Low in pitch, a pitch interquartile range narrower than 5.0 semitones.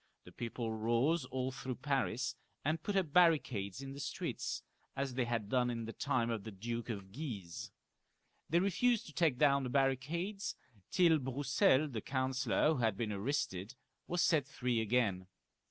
Yes: low, 130 Hz; average, 4.3 semitones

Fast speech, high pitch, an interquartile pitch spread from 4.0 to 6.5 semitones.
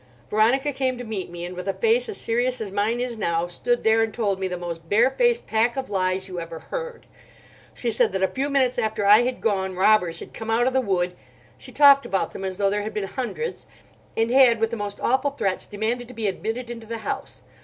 Yes: fast, 230 wpm; high, 220 Hz; average, 4.7 semitones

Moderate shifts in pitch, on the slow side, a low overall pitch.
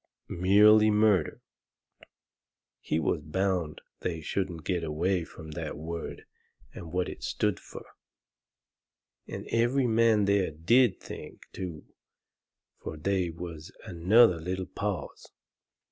Yes: average, 4.0 semitones; slow, 115 wpm; very low, 90 Hz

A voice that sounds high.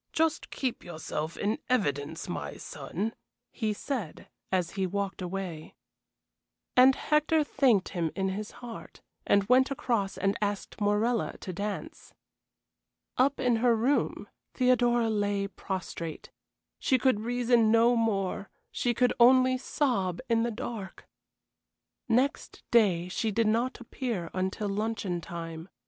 Yes: high, 220 Hz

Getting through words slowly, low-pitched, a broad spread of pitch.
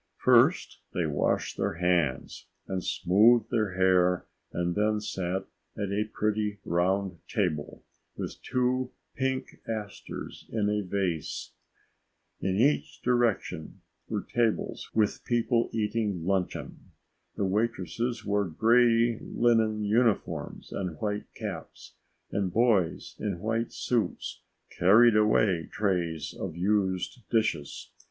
No: slow, 115 wpm; low, 105 Hz; average, 3.8 semitones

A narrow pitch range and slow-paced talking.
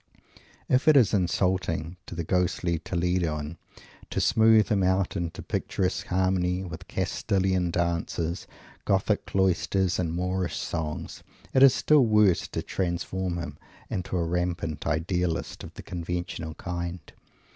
Yes: narrow, 1.8 semitones; slow, 130 wpm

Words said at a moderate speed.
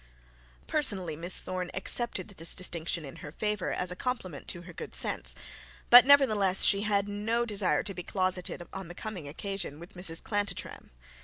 Yes: average, 170 wpm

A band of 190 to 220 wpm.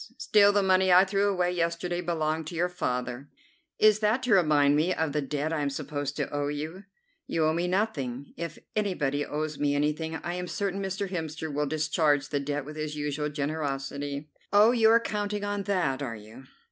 Yes: average, 195 wpm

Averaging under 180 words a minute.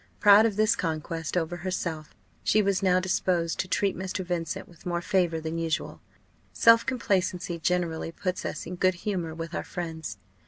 Yes: average, 170 wpm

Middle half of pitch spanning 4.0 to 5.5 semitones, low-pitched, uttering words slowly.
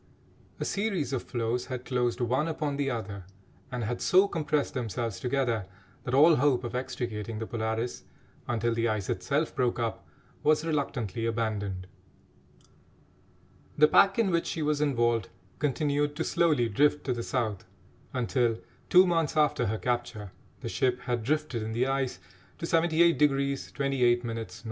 No: average, 4.3 semitones; low, 125 Hz; average, 155 wpm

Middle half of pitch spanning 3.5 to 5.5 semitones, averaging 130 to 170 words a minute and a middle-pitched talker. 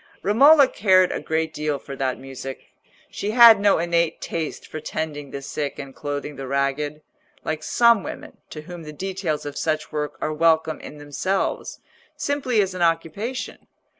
Yes: average, 4.7 semitones; average, 165 wpm; medium, 160 Hz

